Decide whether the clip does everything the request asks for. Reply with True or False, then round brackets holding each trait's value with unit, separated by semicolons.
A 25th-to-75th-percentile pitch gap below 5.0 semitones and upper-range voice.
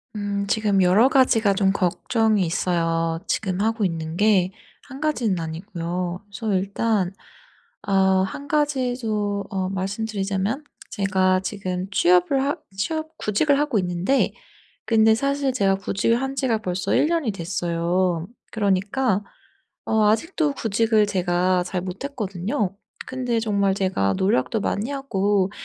True (3.7 semitones; 200 Hz)